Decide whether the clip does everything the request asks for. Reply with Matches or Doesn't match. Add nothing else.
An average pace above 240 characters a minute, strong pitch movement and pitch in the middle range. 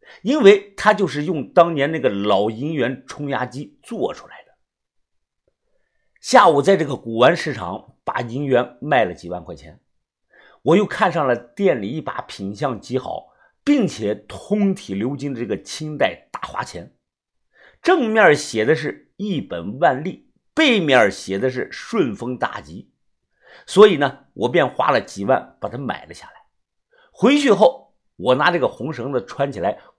Doesn't match